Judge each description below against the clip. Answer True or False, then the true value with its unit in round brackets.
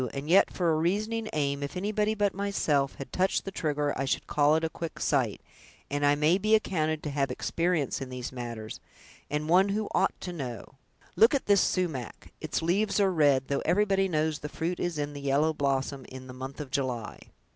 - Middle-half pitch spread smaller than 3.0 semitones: False (5.2 semitones)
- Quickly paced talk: True (210 wpm)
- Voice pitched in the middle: True (155 Hz)